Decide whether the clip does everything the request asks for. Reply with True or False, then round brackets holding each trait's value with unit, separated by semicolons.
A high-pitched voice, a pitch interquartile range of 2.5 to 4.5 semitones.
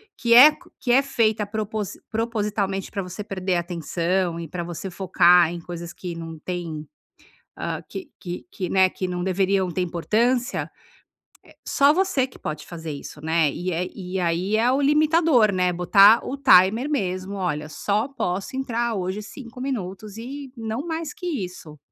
False (195 Hz; 5.1 semitones)